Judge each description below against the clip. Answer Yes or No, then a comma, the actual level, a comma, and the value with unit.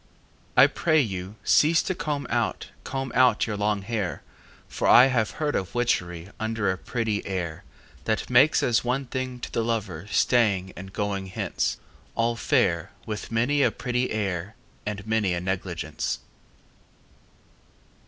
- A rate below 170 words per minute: Yes, average, 150 wpm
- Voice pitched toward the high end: No, low, 110 Hz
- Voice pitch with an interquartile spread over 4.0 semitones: Yes, average, 4.5 semitones